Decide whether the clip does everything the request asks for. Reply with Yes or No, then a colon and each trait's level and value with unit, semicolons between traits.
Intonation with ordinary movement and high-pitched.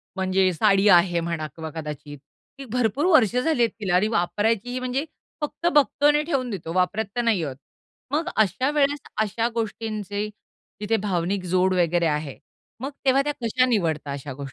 No: wide, 6.5 semitones; high, 210 Hz